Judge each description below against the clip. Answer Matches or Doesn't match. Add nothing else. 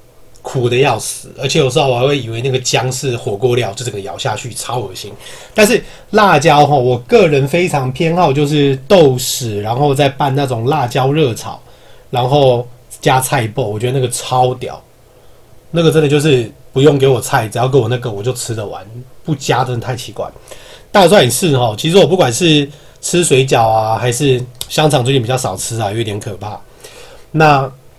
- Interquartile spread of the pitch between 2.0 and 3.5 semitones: Matches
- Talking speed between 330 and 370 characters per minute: Doesn't match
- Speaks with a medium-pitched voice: Doesn't match